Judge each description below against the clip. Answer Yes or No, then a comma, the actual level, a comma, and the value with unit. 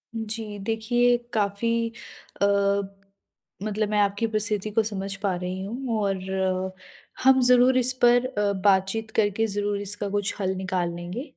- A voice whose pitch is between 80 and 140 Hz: No, high, 210 Hz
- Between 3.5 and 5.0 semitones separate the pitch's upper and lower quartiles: No, narrow, 2.5 semitones